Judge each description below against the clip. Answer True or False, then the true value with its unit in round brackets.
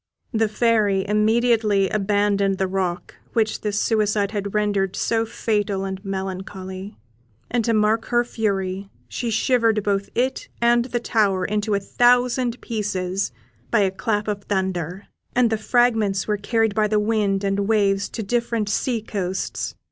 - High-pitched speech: True (210 Hz)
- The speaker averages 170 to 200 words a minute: False (150 wpm)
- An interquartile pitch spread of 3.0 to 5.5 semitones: False (2.4 semitones)